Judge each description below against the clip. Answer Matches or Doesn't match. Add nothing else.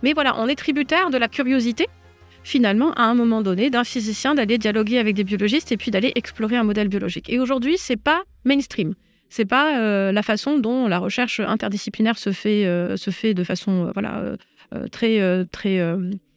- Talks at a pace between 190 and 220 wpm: Matches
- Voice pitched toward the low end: Doesn't match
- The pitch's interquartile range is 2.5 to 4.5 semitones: Matches